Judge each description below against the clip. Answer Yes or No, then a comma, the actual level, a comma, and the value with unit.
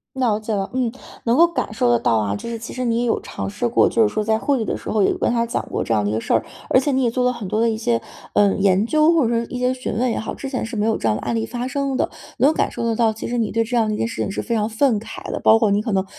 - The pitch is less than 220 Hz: No, high, 225 Hz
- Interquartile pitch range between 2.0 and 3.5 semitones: Yes, average, 3.1 semitones